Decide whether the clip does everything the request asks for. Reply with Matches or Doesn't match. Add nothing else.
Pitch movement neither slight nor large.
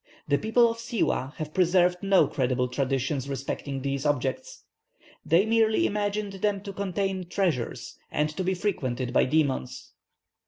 Doesn't match